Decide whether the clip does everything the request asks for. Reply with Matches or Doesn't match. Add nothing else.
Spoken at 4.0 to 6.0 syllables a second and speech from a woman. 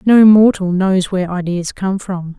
Matches